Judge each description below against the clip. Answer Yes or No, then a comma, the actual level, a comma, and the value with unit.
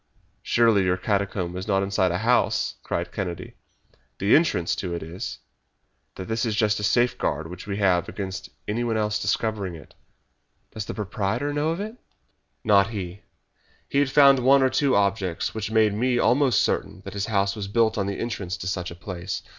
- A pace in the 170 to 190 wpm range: Yes, average, 185 wpm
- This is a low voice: Yes, low, 100 Hz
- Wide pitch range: No, average, 3.8 semitones